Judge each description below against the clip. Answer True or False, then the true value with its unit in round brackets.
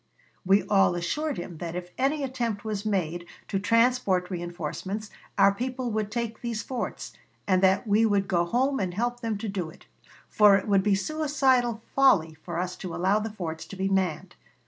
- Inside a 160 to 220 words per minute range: True (190 wpm)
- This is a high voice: True (200 Hz)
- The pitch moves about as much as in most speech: True (4.5 semitones)